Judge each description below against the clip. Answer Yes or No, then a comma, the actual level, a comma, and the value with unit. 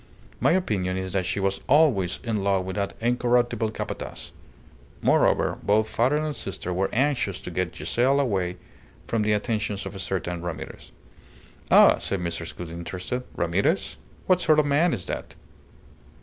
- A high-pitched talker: No, low, 100 Hz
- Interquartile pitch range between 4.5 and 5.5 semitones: Yes, average, 5.2 semitones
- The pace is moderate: Yes, average, 160 wpm